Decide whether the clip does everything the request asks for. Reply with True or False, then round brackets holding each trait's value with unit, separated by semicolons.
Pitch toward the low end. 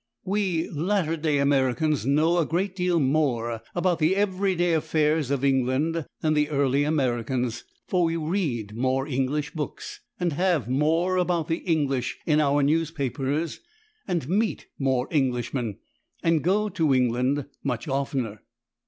False (150 Hz)